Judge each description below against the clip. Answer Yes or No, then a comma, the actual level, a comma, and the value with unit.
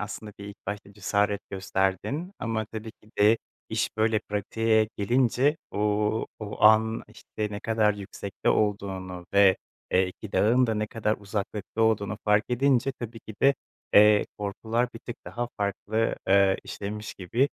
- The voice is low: Yes, low, 105 Hz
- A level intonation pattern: Yes, narrow, 1.8 semitones